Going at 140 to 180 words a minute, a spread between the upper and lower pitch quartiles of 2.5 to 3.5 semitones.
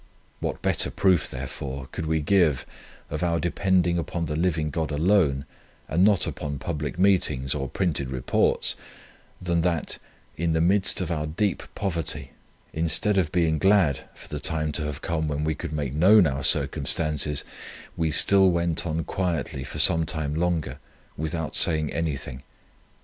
Yes: average, 160 wpm; average, 2.8 semitones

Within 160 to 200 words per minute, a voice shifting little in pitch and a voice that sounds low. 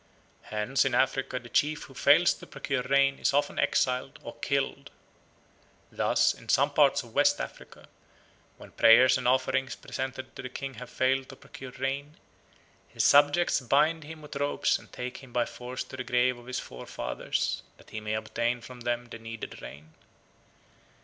Yes: average, 175 wpm; narrow, 2.2 semitones; low, 130 Hz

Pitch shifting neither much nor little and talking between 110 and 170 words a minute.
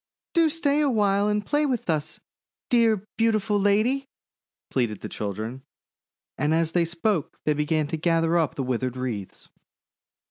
No: wide, 7.2 semitones; average, 150 wpm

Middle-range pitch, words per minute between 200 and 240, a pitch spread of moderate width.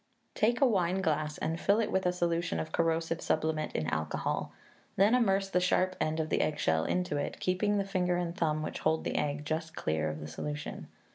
Yes: medium, 165 Hz; fast, 205 wpm; average, 3.4 semitones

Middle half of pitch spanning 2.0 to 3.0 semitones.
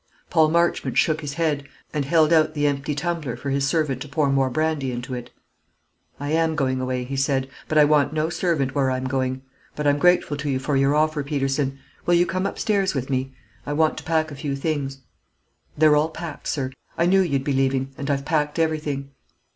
Yes: narrow, 2.6 semitones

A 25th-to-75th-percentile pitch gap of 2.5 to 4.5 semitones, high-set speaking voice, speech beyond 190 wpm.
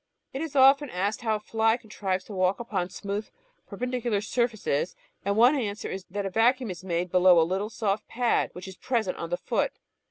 Yes: average, 4.2 semitones; high, 210 Hz; average, 200 wpm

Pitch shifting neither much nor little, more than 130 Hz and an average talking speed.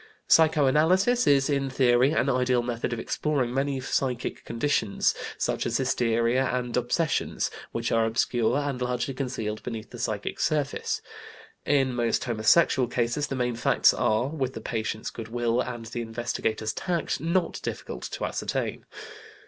No: average, 3.1 semitones; low, 125 Hz; average, 150 wpm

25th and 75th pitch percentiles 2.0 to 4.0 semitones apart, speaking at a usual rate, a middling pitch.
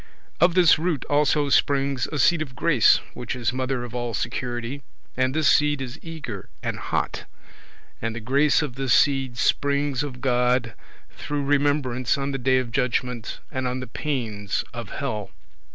No: average, 2.8 semitones; average, 170 wpm; low, 130 Hz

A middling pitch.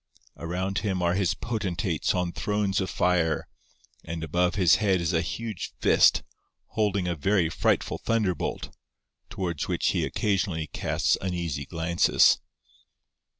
No: very low, 90 Hz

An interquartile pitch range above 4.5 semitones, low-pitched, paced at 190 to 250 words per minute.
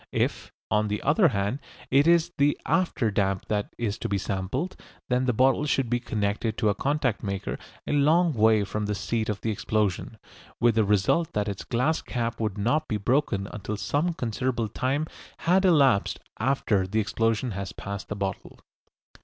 No: average, 5.0 semitones; low, 115 Hz; average, 180 wpm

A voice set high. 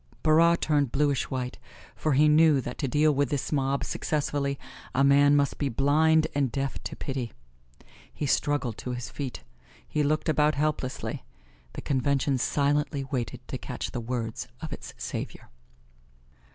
No: medium, 140 Hz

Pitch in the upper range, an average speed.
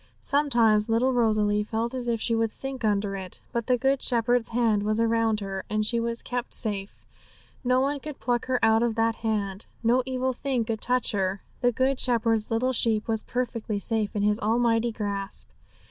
Yes: high, 230 Hz; average, 190 wpm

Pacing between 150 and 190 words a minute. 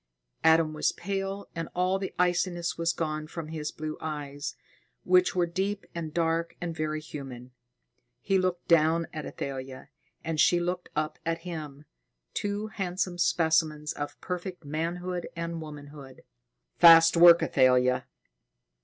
No: slow, 135 wpm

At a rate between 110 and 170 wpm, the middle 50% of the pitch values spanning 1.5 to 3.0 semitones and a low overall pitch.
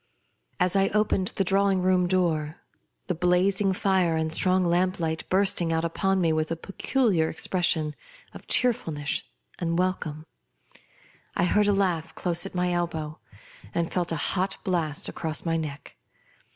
No: average, 155 wpm; average, 2.7 semitones; medium, 180 Hz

